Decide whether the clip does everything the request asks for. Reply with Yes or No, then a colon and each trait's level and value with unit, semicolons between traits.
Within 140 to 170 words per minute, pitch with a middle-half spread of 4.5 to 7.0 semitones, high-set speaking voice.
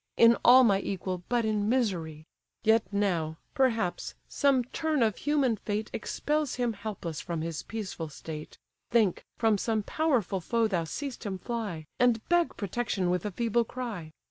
Yes: average, 160 wpm; average, 4.9 semitones; high, 220 Hz